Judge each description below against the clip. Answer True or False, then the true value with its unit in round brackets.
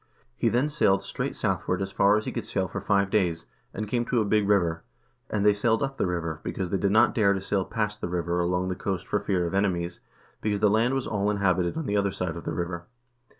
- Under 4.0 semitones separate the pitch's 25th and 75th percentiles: True (3.0 semitones)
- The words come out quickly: True (260 wpm)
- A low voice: True (100 Hz)